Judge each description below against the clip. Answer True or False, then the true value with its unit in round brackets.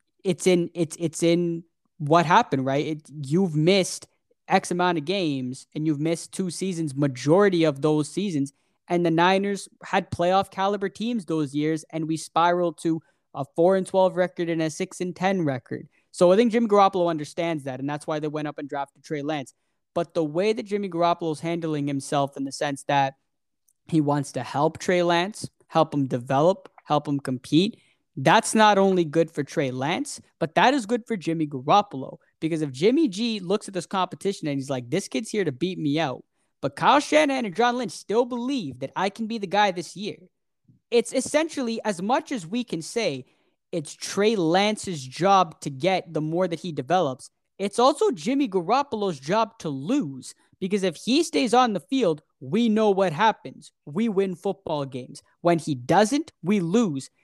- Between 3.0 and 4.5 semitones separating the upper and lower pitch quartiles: False (5.0 semitones)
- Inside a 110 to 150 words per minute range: False (195 wpm)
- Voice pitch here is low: False (175 Hz)